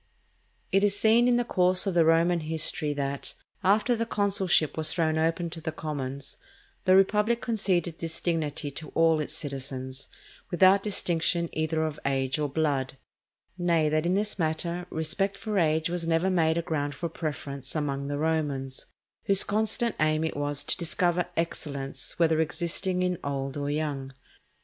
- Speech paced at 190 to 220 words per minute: No, average, 165 wpm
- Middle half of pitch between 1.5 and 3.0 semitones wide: No, average, 3.7 semitones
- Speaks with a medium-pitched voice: Yes, medium, 160 Hz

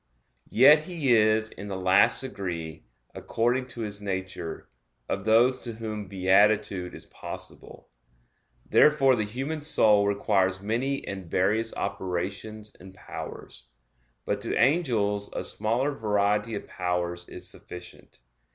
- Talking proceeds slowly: Yes, slow, 125 wpm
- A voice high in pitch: No, low, 105 Hz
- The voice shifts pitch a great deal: No, average, 3.8 semitones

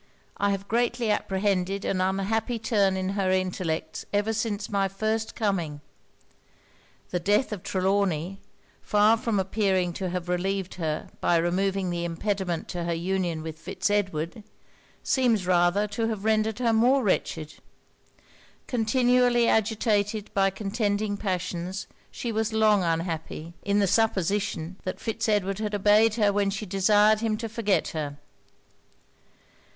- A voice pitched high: Yes, high, 200 Hz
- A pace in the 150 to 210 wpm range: No, average, 140 wpm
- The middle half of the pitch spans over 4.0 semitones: No, average, 2.9 semitones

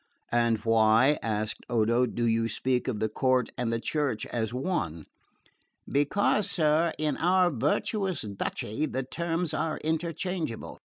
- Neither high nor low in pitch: No, low, 130 Hz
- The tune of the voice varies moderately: No, wide, 6.0 semitones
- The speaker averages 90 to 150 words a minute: Yes, slow, 135 wpm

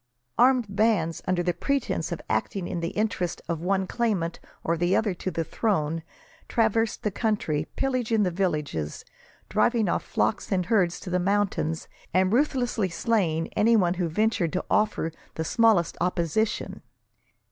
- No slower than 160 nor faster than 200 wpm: No, average, 145 wpm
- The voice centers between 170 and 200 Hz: Yes, medium, 185 Hz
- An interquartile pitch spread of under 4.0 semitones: No, average, 4.7 semitones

